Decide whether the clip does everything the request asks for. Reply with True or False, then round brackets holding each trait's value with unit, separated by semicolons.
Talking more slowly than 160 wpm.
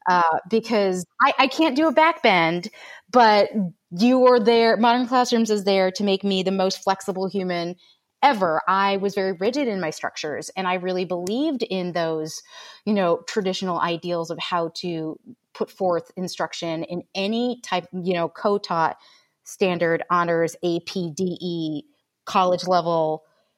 True (150 wpm)